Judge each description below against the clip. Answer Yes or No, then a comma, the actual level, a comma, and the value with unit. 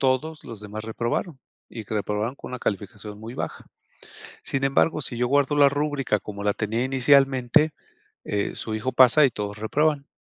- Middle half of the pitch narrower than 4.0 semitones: No, average, 4.6 semitones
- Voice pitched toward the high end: No, low, 125 Hz